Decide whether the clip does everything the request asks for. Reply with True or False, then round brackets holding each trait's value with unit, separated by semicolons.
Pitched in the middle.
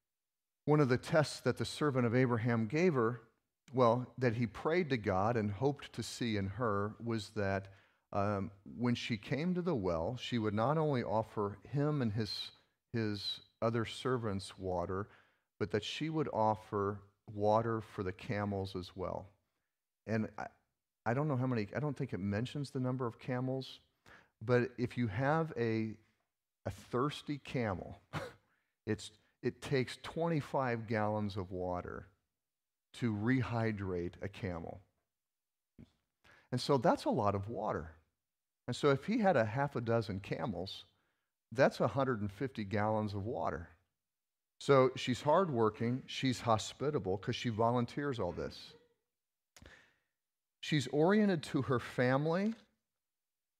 False (115 Hz)